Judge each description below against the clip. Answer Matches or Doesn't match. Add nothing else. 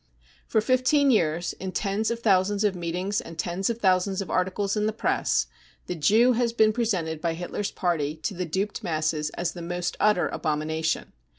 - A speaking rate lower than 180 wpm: Doesn't match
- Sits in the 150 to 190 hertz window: Matches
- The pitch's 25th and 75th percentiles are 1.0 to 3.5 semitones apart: Doesn't match